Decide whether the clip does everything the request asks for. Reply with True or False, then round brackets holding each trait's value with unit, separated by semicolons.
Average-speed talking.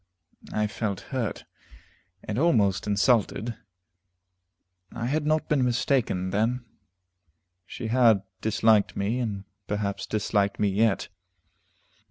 False (105 wpm)